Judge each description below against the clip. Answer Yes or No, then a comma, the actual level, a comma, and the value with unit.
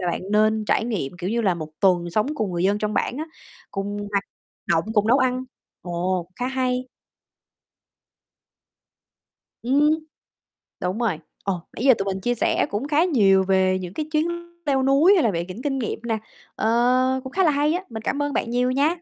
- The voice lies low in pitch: No, high, 225 Hz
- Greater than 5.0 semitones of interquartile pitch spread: Yes, wide, 5.6 semitones